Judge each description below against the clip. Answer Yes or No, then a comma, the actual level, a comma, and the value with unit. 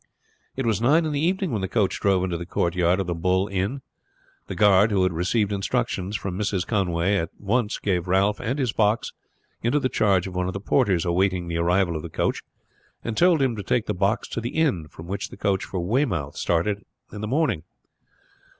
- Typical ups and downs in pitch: Yes, average, 4.1 semitones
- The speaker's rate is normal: No, fast, 215 wpm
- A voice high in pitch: No, low, 100 Hz